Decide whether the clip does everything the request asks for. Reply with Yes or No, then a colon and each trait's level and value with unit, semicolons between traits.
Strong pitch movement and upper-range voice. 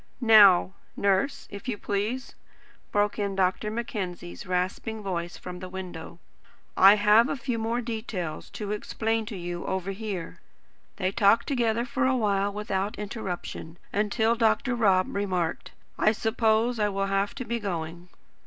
No: average, 3.1 semitones; high, 205 Hz